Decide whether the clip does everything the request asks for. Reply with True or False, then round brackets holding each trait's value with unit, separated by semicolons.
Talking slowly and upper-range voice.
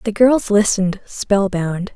True (125 wpm; 200 Hz)